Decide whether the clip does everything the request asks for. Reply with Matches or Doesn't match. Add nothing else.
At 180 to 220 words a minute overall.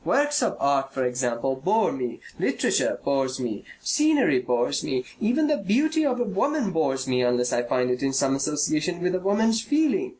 Matches